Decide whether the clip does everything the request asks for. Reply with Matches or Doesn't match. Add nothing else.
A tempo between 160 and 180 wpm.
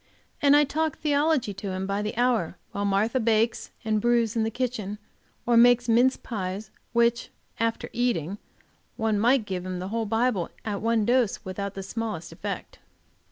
Matches